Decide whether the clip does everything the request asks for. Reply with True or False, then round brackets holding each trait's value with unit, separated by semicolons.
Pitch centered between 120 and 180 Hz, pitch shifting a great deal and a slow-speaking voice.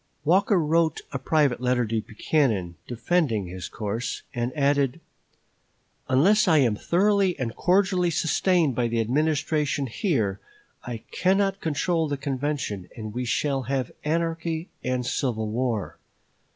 True (140 Hz; 5.7 semitones; 130 wpm)